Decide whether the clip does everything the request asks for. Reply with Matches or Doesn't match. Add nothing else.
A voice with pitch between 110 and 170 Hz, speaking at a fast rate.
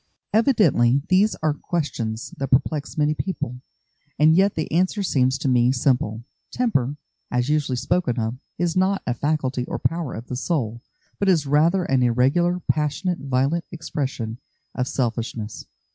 Doesn't match